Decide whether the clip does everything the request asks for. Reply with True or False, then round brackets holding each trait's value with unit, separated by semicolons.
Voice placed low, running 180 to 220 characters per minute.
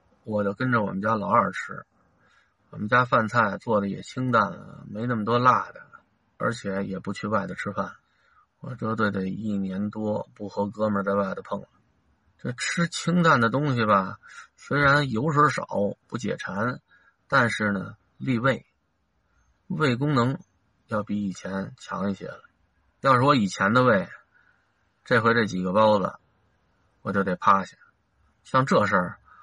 True (105 Hz; 215 characters per minute)